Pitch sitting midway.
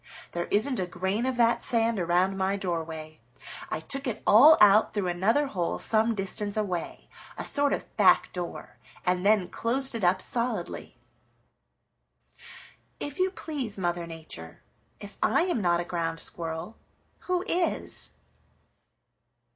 No: high, 200 Hz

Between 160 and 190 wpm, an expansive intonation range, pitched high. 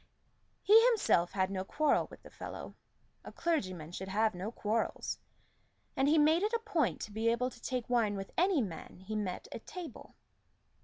Yes: average, 185 wpm; wide, 8.1 semitones; high, 230 Hz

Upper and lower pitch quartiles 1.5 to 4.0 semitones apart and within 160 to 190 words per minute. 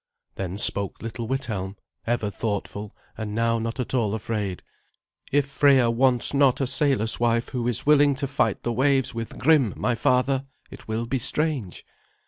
Yes: average, 3.4 semitones; average, 165 wpm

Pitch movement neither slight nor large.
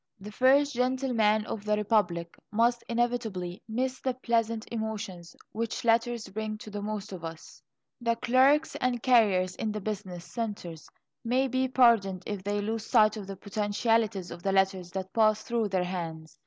Yes: average, 3.6 semitones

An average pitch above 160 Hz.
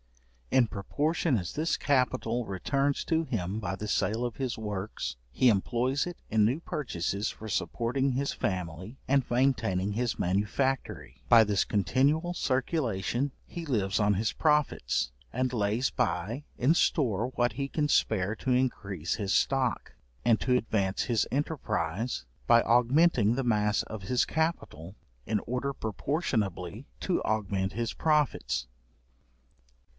No: low, 115 Hz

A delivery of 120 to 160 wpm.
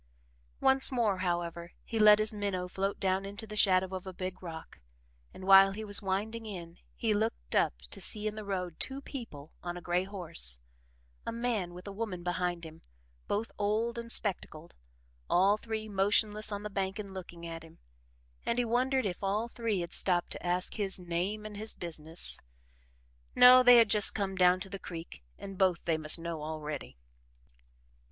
No: average, 185 wpm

